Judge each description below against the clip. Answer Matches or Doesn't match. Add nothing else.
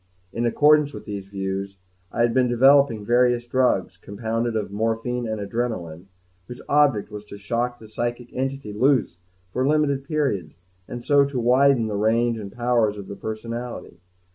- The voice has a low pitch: Matches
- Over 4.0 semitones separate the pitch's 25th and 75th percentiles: Doesn't match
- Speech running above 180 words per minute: Doesn't match